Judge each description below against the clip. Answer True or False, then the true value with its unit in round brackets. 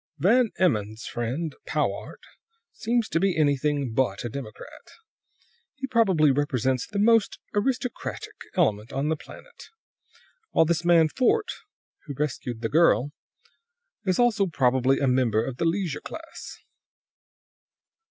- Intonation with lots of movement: True (7.7 semitones)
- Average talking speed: False (125 wpm)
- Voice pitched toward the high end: False (150 Hz)